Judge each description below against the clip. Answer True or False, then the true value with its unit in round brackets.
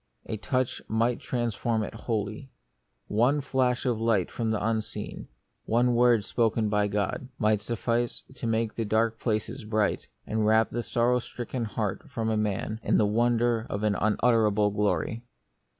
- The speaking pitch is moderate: False (115 Hz)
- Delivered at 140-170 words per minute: True (155 wpm)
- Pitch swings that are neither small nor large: False (1.9 semitones)